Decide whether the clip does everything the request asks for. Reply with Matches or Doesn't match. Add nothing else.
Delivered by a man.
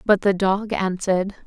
Doesn't match